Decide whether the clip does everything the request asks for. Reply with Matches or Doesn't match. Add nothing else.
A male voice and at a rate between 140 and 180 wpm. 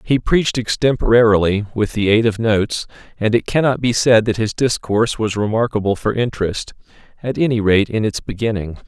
Matches